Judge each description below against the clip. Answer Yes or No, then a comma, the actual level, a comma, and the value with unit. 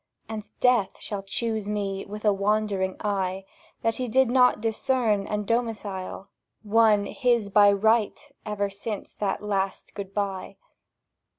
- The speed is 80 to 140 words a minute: Yes, slow, 135 wpm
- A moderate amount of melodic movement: No, narrow, 2.2 semitones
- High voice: Yes, high, 210 Hz